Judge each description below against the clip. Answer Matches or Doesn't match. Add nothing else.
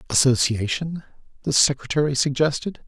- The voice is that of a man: Matches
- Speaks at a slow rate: Matches